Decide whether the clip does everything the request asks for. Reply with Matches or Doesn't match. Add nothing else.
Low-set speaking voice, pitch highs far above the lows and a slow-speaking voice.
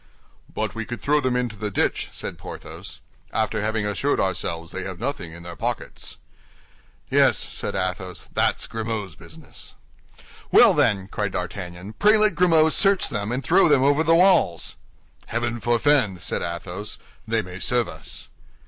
Doesn't match